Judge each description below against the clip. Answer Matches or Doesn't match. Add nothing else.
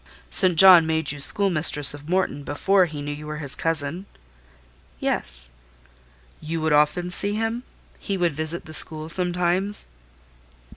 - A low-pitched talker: Doesn't match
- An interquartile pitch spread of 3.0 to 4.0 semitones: Matches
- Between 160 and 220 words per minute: Doesn't match